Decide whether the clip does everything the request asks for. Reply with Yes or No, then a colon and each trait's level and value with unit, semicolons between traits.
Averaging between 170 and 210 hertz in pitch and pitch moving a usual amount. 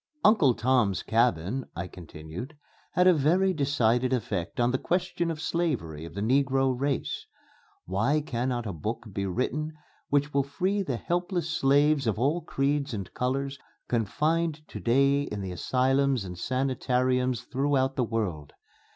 No: low, 130 Hz; average, 4.3 semitones